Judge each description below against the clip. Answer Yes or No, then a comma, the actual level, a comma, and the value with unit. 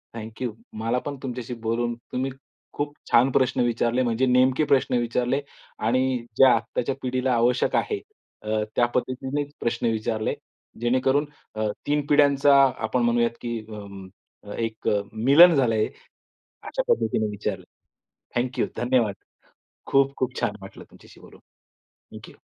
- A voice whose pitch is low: Yes, low, 125 Hz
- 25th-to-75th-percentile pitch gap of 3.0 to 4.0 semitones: No, narrow, 2.6 semitones